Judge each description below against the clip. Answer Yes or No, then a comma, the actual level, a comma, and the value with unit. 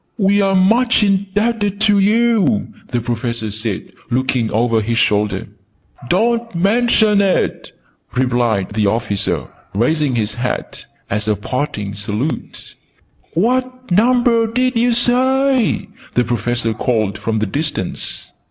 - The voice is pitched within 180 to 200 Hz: No, medium, 150 Hz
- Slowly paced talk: Yes, slow, 120 wpm